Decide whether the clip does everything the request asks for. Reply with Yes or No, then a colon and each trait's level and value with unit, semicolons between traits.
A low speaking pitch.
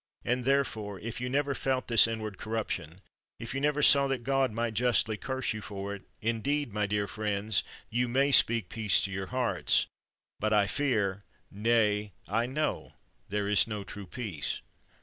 Yes: low, 110 Hz